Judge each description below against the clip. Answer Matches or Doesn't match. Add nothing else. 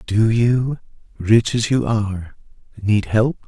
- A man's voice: Matches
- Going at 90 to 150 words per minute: Matches